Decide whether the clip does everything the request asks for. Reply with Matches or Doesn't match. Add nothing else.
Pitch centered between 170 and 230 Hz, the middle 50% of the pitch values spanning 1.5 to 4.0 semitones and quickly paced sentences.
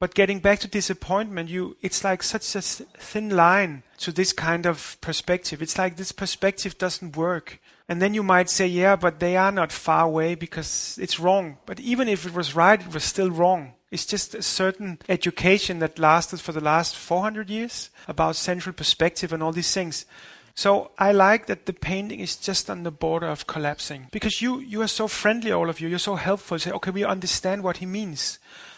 Matches